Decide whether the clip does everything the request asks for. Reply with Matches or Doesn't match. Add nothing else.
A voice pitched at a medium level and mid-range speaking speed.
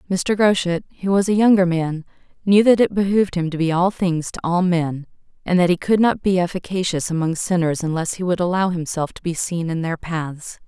Doesn't match